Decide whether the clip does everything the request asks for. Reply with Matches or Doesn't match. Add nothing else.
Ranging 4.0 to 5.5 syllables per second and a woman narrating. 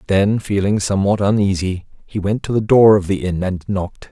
Doesn't match